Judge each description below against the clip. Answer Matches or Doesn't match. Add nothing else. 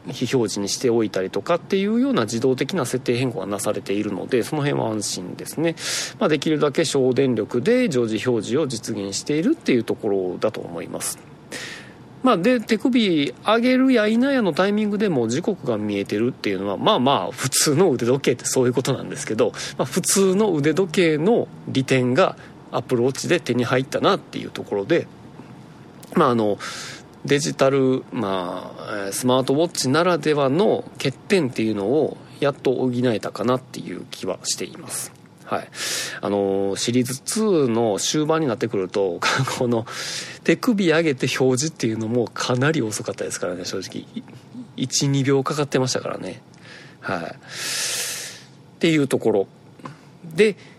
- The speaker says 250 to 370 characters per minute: Matches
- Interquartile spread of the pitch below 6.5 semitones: Matches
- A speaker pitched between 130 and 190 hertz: Matches